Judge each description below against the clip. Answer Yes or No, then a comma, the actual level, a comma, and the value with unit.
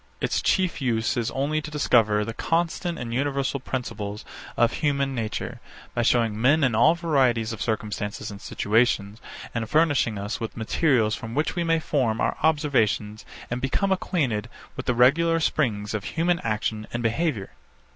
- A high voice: No, low, 125 Hz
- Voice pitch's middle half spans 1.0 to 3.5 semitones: No, wide, 5.5 semitones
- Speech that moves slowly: No, average, 165 wpm